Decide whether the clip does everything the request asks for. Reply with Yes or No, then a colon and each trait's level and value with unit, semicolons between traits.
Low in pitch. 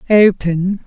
No: high, 190 Hz